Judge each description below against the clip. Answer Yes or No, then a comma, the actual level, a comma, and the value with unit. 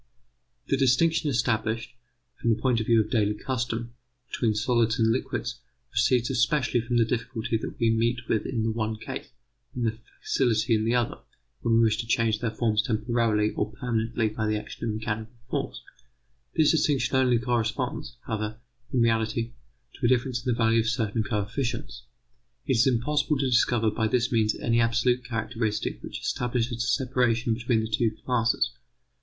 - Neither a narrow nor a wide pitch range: No, narrow, 1.8 semitones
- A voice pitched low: Yes, low, 115 Hz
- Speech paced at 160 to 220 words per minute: Yes, average, 175 wpm